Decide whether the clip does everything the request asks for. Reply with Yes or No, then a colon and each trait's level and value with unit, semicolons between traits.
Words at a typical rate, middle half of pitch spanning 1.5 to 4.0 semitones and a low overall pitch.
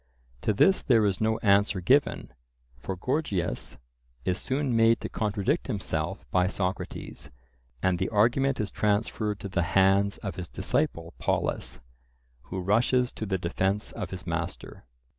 Yes: average, 145 wpm; average, 3.4 semitones; low, 100 Hz